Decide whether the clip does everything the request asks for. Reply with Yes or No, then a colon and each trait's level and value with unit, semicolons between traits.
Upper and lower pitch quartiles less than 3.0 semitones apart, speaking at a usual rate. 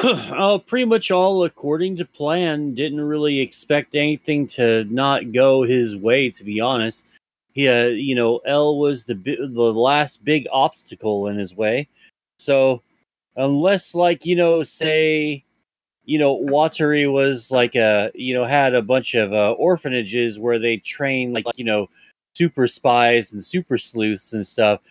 No: average, 4.3 semitones; average, 160 wpm